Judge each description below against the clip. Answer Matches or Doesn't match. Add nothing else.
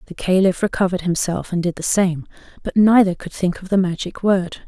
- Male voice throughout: Doesn't match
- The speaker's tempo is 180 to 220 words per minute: Matches